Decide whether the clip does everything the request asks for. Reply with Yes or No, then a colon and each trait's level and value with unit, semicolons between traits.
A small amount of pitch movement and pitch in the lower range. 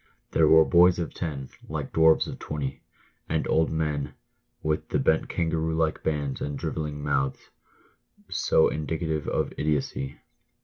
Yes: narrow, 1.8 semitones; very low, 80 Hz